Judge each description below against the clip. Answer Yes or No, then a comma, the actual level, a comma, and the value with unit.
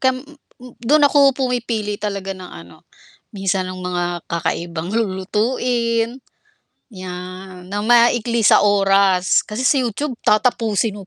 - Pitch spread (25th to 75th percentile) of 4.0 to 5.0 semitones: Yes, average, 4.4 semitones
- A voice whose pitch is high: Yes, high, 205 Hz